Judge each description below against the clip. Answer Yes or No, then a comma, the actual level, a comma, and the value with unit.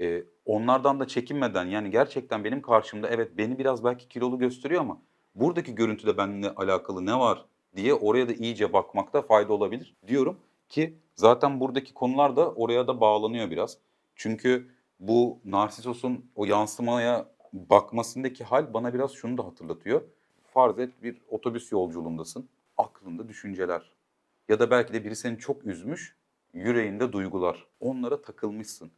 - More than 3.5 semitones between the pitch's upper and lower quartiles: No, average, 3.0 semitones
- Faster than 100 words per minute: Yes, fast, 140 wpm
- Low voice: Yes, low, 120 Hz